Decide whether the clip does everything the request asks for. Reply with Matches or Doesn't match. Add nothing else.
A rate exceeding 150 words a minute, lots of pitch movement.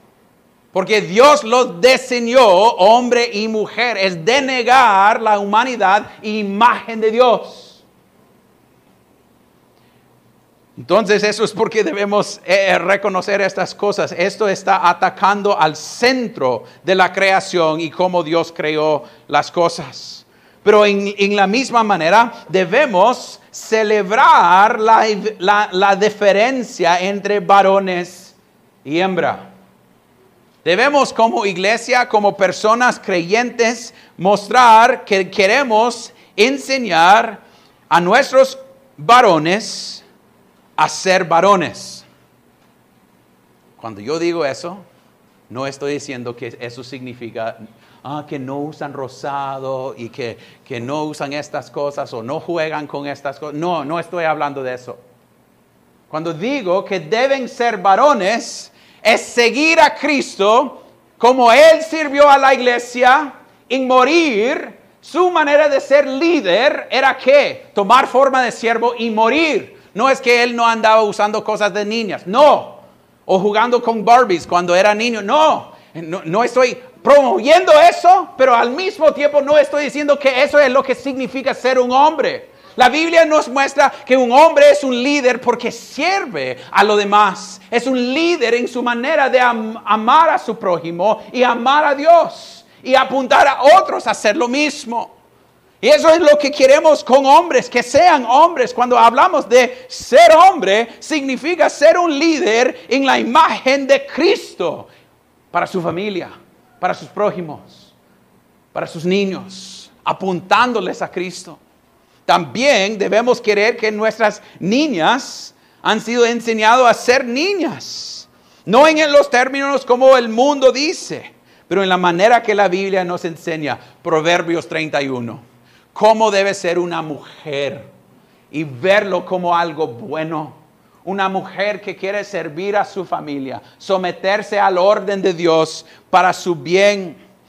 Doesn't match